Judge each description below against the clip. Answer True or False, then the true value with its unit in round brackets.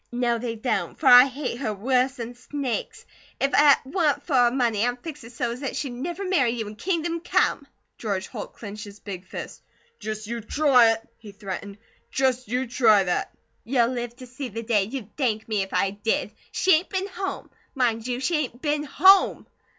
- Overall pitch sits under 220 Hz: False (245 Hz)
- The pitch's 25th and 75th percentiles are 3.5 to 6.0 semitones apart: True (4.0 semitones)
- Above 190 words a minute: True (200 wpm)